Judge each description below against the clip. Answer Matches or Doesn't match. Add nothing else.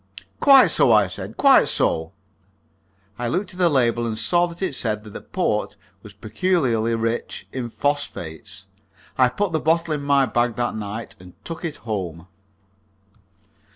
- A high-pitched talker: Doesn't match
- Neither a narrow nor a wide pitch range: Doesn't match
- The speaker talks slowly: Doesn't match